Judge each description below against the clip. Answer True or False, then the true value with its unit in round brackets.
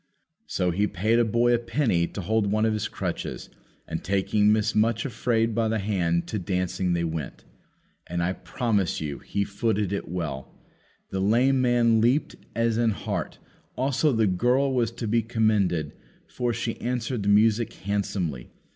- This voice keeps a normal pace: True (170 wpm)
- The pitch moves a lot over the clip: False (4.0 semitones)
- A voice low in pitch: True (110 Hz)